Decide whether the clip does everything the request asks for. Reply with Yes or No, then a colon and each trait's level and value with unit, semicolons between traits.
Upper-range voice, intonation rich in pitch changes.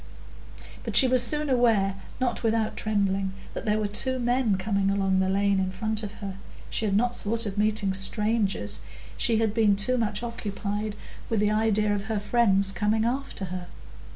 No: high, 210 Hz; narrow, 2.4 semitones